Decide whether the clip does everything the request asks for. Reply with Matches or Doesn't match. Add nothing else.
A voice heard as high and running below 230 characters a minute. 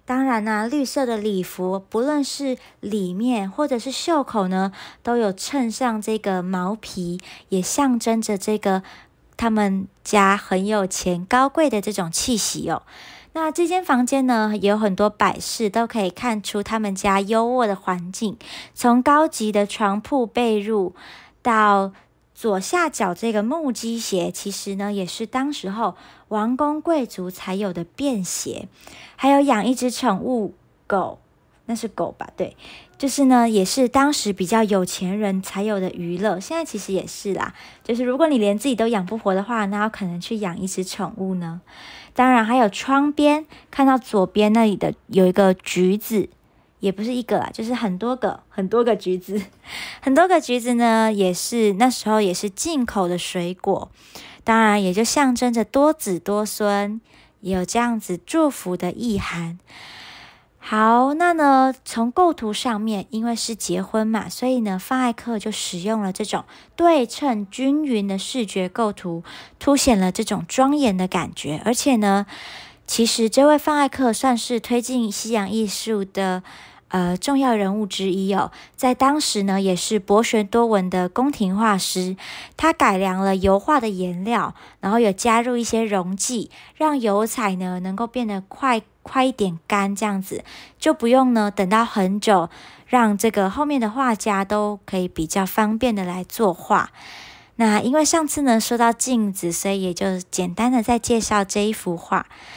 Doesn't match